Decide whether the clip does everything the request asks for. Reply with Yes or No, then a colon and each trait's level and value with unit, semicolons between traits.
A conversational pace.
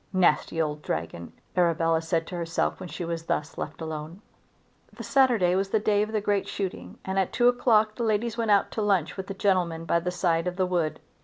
No: fast, 220 wpm